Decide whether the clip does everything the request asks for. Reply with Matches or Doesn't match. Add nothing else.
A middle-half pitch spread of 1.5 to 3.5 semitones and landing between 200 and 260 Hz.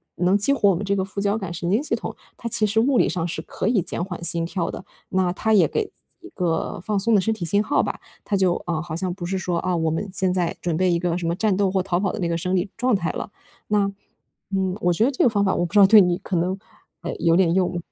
Doesn't match